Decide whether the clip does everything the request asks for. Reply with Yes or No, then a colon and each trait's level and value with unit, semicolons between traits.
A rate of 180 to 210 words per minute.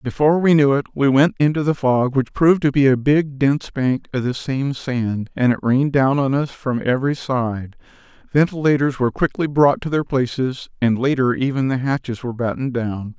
Yes: fast, 205 wpm